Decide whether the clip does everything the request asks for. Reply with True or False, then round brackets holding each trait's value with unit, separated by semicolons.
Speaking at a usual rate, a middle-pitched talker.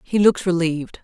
True (175 wpm; 175 Hz)